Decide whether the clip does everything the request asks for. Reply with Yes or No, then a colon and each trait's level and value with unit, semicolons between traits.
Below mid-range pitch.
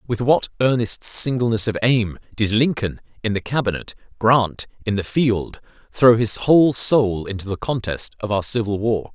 Yes: low, 115 Hz